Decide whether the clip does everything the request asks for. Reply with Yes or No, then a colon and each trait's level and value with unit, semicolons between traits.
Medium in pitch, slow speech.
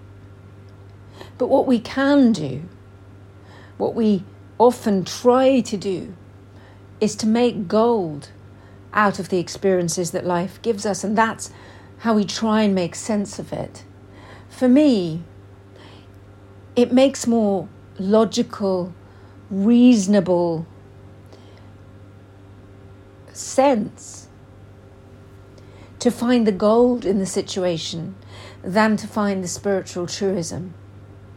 Yes: medium, 165 Hz; slow, 105 wpm